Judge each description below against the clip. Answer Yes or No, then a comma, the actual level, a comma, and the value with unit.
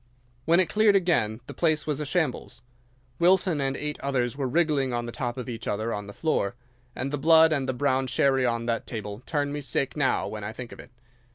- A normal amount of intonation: Yes, average, 4.5 semitones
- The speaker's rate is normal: No, fast, 225 wpm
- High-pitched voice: No, low, 135 Hz